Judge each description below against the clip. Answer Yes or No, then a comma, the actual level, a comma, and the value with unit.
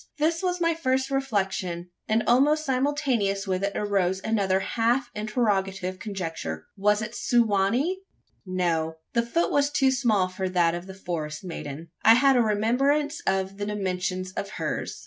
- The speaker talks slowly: No, average, 165 wpm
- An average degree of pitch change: No, wide, 5.8 semitones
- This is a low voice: No, high, 210 Hz